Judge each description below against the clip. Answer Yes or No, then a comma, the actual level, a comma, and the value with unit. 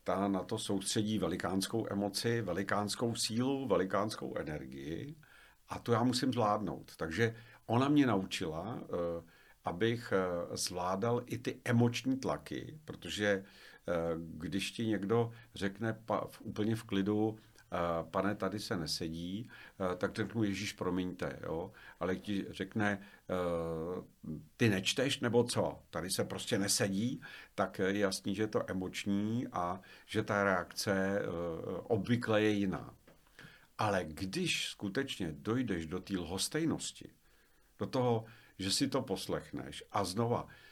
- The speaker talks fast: No, average, 120 wpm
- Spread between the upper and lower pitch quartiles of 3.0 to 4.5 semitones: Yes, average, 3.4 semitones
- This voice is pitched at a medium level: No, low, 100 Hz